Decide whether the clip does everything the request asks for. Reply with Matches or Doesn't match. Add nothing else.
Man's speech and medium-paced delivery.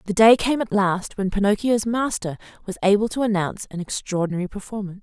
Doesn't match